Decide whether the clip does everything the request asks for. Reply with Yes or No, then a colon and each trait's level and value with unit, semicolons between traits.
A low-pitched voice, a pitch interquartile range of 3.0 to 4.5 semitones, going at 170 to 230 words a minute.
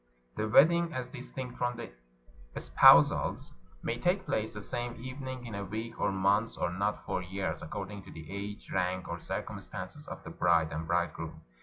No: low, 105 Hz; average, 4.9 semitones; average, 175 wpm